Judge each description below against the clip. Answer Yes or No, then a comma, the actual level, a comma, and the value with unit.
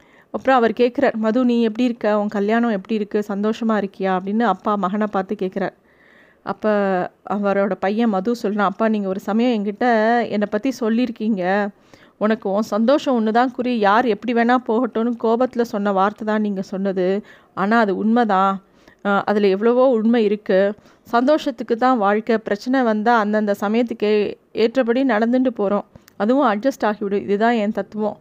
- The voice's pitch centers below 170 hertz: No, high, 215 Hz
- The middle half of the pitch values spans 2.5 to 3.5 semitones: Yes, average, 2.8 semitones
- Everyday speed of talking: No, fast, 145 wpm